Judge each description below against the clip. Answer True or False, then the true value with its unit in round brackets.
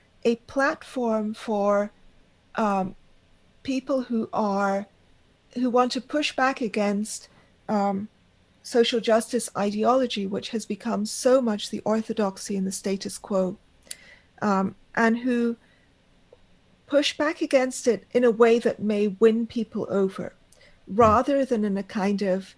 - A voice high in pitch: True (220 Hz)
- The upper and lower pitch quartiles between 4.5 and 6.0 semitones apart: False (3.2 semitones)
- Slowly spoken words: True (130 wpm)